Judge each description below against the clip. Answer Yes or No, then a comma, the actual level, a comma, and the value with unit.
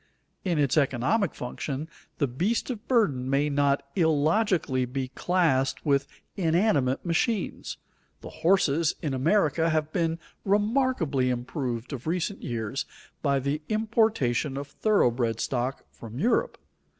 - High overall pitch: No, medium, 150 Hz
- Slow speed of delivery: Yes, slow, 125 wpm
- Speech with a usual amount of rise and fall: No, wide, 6.0 semitones